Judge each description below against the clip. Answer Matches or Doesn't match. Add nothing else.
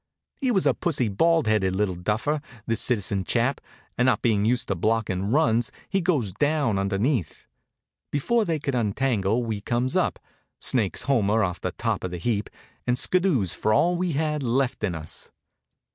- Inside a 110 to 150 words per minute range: Doesn't match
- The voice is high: Doesn't match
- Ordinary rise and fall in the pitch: Doesn't match